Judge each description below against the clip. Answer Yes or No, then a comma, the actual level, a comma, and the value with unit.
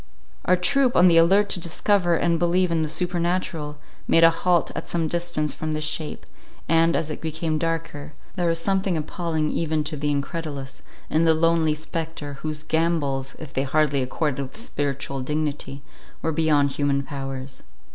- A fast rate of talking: No, average, 170 wpm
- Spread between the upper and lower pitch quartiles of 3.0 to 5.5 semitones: No, narrow, 2.4 semitones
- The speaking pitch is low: No, medium, 160 Hz